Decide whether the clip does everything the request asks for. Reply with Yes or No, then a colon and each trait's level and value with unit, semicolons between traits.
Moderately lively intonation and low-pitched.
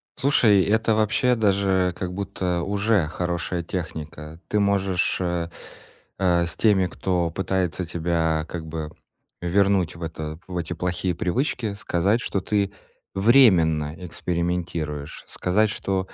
Yes: average, 3.1 semitones; very low, 90 Hz